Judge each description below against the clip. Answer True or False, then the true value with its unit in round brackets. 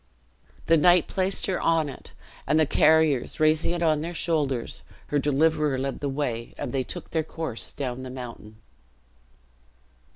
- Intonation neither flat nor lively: True (3.4 semitones)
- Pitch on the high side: False (150 Hz)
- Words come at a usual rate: True (160 wpm)